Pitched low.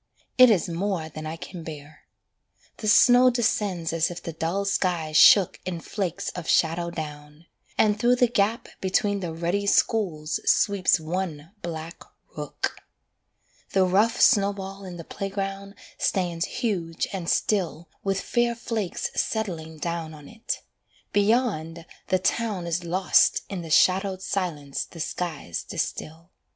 No: medium, 180 Hz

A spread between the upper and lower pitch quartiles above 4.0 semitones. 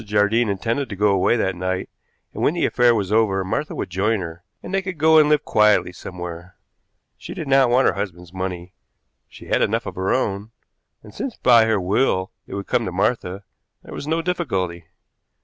Yes: average, 5.1 semitones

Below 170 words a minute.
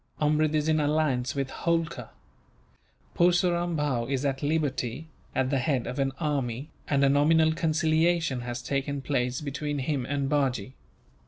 Yes: average, 150 wpm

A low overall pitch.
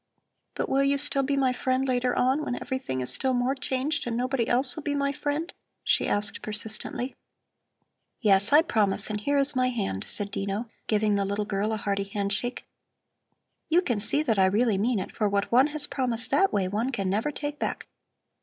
No: high, 245 Hz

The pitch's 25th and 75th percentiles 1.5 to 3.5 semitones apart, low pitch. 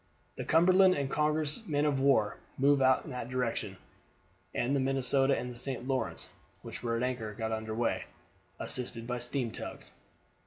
Yes: average, 3.0 semitones; low, 130 Hz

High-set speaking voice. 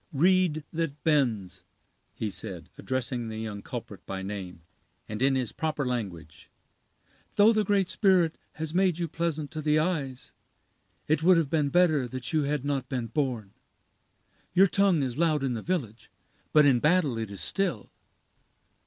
No: medium, 145 Hz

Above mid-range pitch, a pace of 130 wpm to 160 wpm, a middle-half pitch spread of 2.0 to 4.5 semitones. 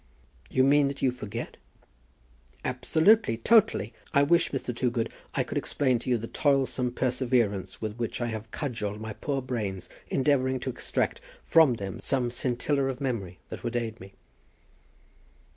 No: low, 125 Hz; average, 155 wpm; average, 3.3 semitones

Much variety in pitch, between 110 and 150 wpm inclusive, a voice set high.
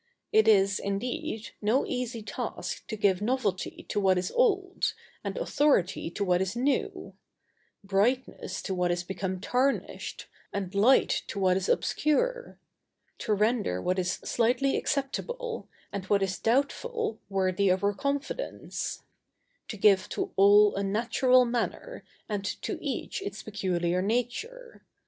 Yes: wide, 5.9 semitones; average, 140 wpm; high, 215 Hz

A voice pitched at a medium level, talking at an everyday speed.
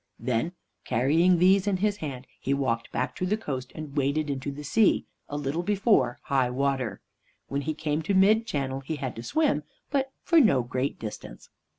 Yes: medium, 145 Hz; average, 190 wpm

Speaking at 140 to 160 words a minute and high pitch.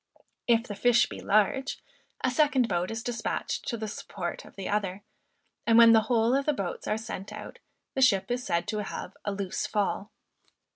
No: average, 195 wpm; high, 220 Hz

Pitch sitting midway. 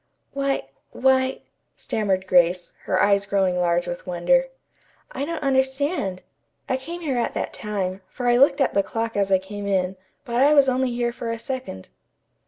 No: high, 230 Hz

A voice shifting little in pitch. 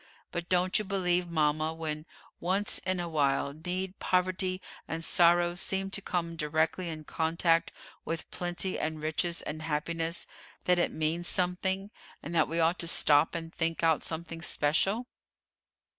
Yes: narrow, 2.2 semitones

